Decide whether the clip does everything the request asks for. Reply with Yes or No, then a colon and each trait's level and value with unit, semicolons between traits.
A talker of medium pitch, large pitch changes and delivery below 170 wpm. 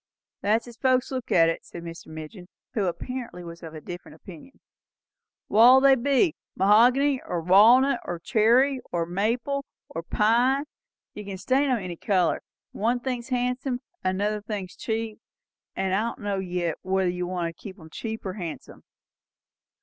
No: high, 210 Hz; wide, 5.9 semitones; average, 160 wpm